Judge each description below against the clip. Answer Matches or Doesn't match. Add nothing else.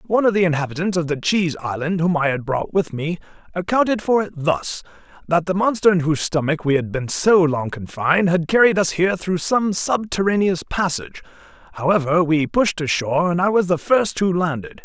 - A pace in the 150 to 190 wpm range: Doesn't match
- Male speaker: Matches